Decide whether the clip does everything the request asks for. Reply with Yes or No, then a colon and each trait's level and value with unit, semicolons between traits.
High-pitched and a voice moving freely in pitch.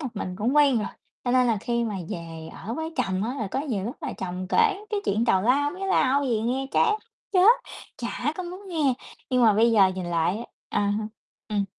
Yes: high, 235 Hz; wide, 5.9 semitones